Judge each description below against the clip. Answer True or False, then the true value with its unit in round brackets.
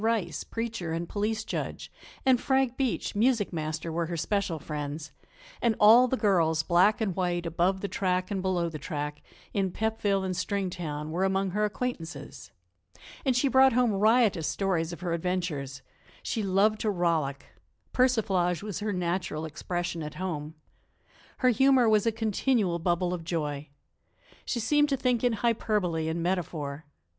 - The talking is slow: False (160 wpm)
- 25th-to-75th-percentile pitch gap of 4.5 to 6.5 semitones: True (4.9 semitones)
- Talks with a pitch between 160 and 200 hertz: True (185 Hz)